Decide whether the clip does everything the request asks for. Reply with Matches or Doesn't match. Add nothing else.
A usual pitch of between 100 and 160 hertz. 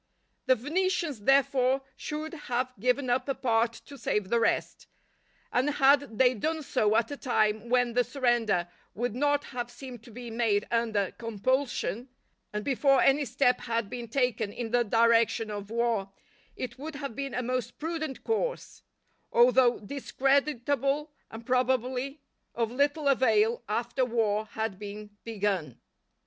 Doesn't match